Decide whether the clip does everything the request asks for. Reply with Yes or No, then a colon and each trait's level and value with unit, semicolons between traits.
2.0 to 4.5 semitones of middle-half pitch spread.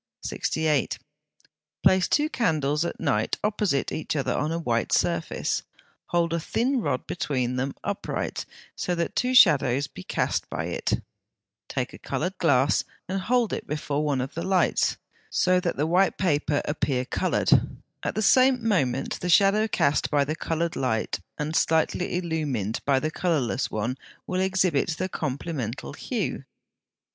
No: average, 5.1 semitones